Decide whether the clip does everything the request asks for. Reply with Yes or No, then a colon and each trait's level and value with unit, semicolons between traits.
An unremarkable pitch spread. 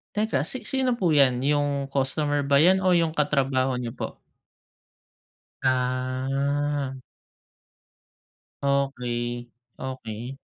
No: narrow, 2.3 semitones